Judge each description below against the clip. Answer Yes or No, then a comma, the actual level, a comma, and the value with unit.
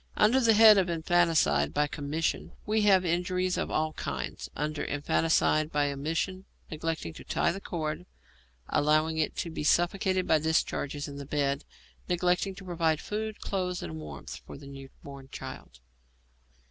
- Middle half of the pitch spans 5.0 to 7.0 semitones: No, average, 4.0 semitones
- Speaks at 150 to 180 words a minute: Yes, average, 160 wpm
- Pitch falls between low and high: Yes, medium, 160 Hz